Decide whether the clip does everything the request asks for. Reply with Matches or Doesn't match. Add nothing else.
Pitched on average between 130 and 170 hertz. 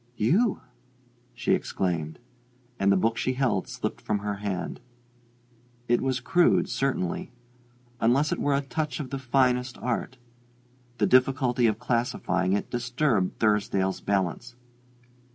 Doesn't match